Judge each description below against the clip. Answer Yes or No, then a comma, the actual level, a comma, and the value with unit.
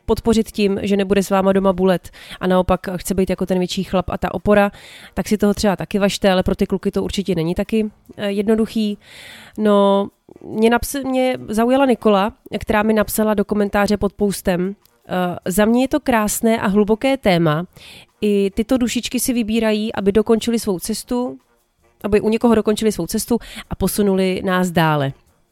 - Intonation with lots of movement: No, average, 2.7 semitones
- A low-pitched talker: No, high, 205 Hz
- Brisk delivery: Yes, fast, 175 wpm